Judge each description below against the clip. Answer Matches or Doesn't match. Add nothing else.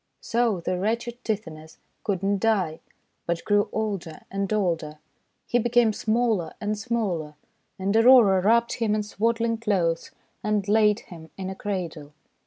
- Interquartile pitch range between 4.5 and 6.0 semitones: Doesn't match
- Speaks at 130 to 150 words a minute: Matches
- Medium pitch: Doesn't match